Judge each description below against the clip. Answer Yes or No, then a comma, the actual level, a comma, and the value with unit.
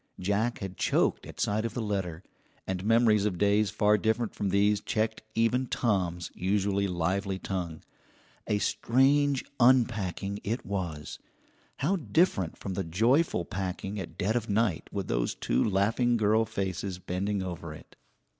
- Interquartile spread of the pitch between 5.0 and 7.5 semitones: No, average, 3.2 semitones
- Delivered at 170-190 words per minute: No, average, 150 wpm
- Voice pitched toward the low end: Yes, low, 100 Hz